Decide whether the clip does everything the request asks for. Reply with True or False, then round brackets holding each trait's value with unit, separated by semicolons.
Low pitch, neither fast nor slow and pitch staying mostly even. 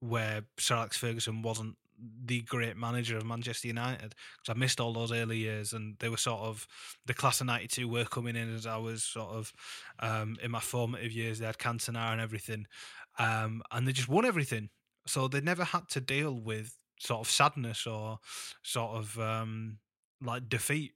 True (115 Hz; 195 wpm; 1.7 semitones)